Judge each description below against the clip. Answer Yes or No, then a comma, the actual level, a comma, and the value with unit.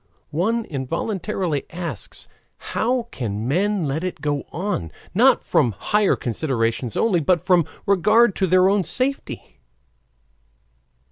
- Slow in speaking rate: Yes, slow, 120 wpm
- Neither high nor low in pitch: Yes, medium, 175 Hz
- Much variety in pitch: Yes, wide, 6.8 semitones